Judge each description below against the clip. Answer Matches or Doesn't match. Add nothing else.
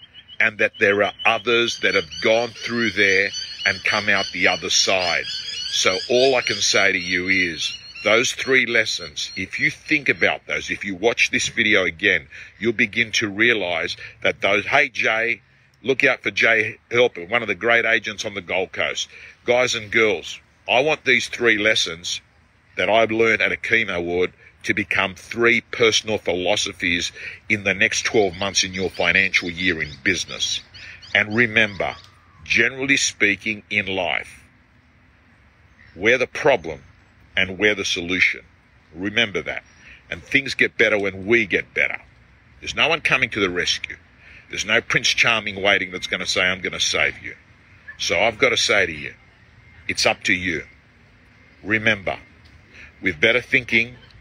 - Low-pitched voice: Matches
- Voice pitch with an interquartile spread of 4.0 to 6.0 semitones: Doesn't match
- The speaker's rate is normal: Matches